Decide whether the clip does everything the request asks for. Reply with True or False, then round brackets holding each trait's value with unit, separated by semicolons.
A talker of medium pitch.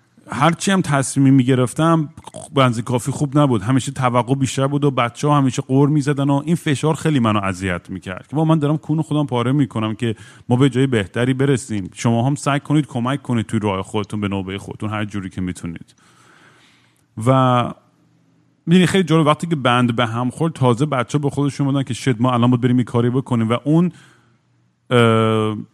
False (130 Hz)